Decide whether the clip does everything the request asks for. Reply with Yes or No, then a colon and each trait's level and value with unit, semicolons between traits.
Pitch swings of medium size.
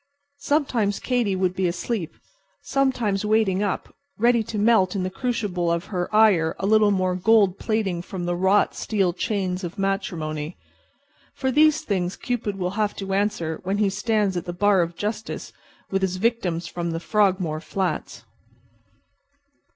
Yes: average, 3.2 semitones